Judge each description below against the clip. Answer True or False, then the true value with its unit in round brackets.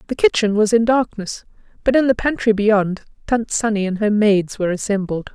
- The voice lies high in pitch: True (215 Hz)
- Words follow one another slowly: False (190 wpm)